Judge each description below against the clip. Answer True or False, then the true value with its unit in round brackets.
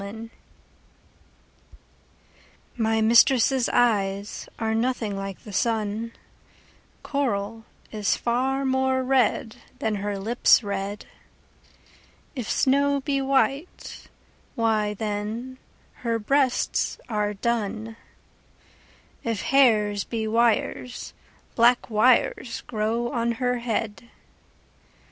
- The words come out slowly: True (90 wpm)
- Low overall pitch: False (230 Hz)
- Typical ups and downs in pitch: True (3.1 semitones)